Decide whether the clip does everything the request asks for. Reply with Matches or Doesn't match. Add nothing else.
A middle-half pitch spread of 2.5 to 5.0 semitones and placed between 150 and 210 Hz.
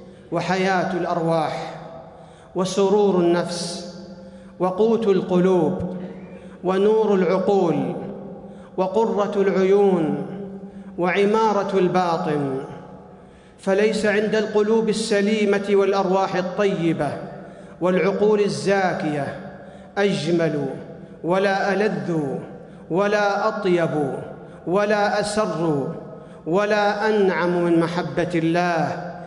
Matches